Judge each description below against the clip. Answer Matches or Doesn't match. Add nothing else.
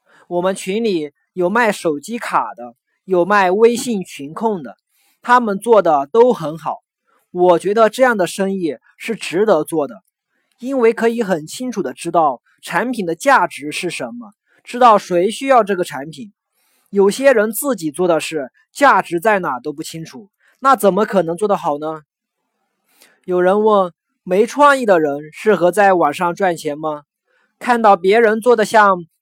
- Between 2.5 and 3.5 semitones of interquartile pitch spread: Doesn't match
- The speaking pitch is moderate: Doesn't match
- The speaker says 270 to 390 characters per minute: Doesn't match